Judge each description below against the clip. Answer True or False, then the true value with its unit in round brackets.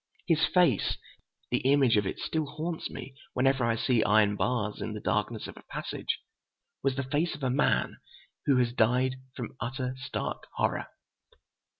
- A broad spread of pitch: False (3.5 semitones)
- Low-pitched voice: True (130 Hz)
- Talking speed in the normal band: True (160 wpm)